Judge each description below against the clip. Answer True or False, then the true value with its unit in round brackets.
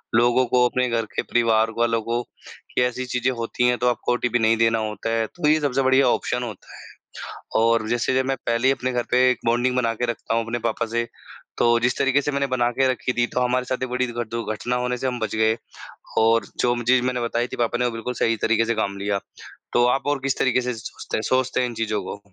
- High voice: False (120 Hz)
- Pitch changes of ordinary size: False (1.7 semitones)